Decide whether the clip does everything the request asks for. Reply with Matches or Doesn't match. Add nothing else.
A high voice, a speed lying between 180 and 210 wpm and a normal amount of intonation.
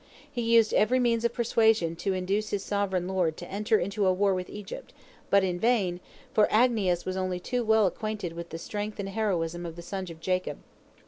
Matches